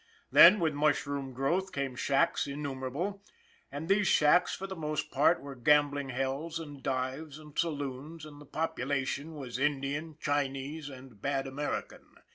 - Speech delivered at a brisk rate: No, average, 145 wpm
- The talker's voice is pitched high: No, medium, 145 Hz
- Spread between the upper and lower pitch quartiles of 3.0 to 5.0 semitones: No, narrow, 2.4 semitones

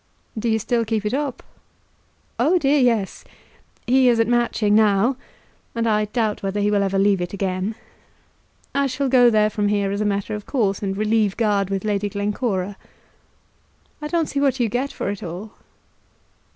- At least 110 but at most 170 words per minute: No, average, 180 wpm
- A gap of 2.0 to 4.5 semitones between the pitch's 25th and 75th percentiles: Yes, average, 3.2 semitones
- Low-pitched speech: No, high, 215 Hz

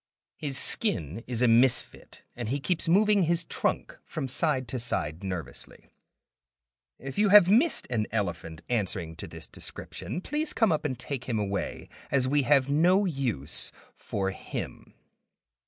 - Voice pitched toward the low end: Yes, low, 130 Hz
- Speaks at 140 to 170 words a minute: Yes, average, 155 wpm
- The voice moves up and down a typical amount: No, wide, 8.2 semitones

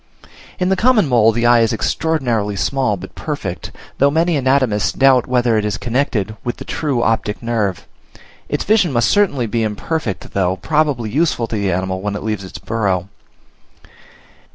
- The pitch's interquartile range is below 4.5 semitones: No, average, 5.2 semitones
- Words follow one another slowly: No, average, 170 wpm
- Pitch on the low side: Yes, low, 115 Hz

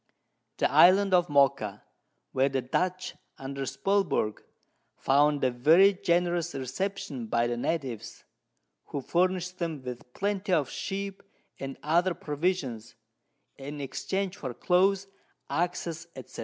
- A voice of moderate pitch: Yes, medium, 160 Hz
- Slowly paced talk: Yes, slow, 120 wpm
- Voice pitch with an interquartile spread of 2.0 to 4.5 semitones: No, wide, 5.5 semitones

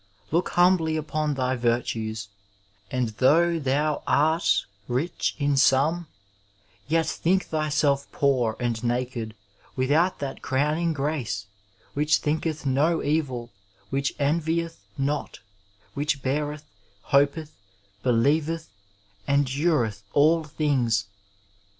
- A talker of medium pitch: Yes, medium, 145 Hz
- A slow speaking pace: Yes, slow, 100 wpm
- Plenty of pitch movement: No, average, 3.4 semitones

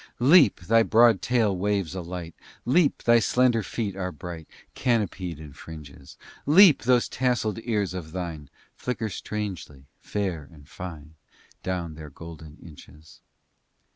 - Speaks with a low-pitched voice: Yes, very low, 95 Hz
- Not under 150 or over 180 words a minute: No, average, 140 wpm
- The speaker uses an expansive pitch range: Yes, wide, 6.1 semitones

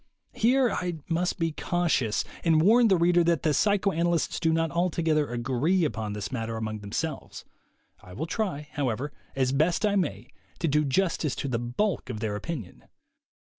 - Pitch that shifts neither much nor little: No, wide, 6.2 semitones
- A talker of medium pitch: Yes, medium, 160 Hz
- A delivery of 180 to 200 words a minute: No, average, 170 wpm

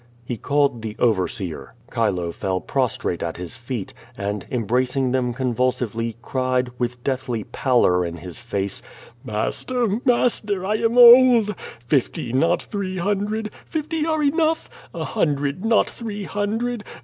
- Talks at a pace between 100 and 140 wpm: Yes, slow, 135 wpm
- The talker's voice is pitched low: Yes, low, 130 Hz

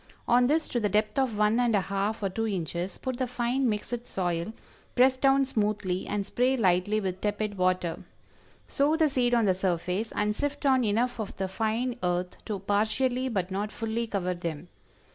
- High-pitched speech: Yes, high, 215 Hz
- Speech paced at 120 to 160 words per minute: No, average, 190 wpm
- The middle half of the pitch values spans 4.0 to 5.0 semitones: Yes, average, 4.4 semitones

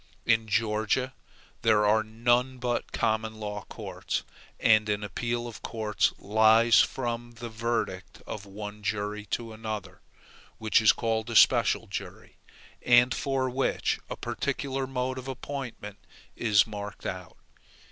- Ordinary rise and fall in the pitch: No, narrow, 2.3 semitones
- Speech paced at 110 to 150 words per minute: Yes, slow, 135 wpm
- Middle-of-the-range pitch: No, low, 110 Hz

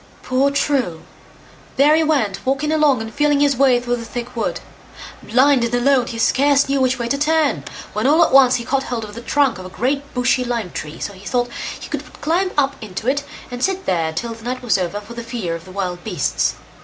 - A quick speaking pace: Yes, fast, 230 wpm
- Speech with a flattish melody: No, average, 4.2 semitones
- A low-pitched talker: No, very high, 250 Hz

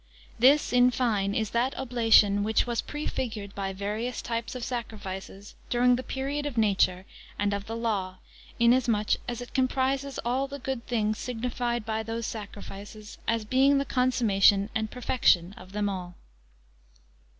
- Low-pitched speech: No, high, 230 Hz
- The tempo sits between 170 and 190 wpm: No, average, 160 wpm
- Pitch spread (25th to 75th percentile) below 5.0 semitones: Yes, average, 3.5 semitones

